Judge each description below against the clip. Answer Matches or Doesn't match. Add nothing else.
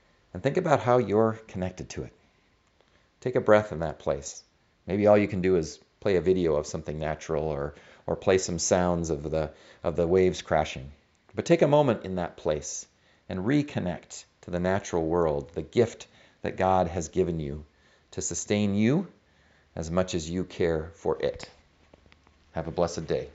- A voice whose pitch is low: Matches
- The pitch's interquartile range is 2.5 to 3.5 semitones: Doesn't match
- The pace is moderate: Matches